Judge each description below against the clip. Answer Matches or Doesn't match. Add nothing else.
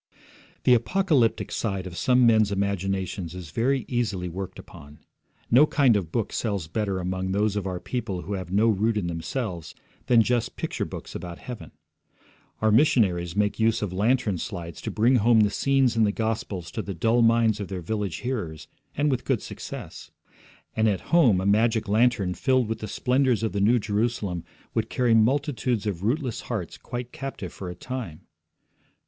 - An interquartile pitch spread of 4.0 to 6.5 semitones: Matches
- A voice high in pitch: Doesn't match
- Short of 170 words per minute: Doesn't match